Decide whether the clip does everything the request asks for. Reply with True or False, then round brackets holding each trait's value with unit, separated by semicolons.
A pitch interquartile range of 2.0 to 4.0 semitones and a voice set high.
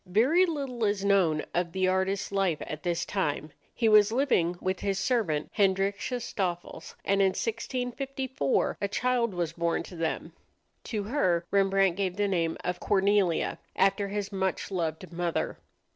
True (3.2 semitones; 195 Hz)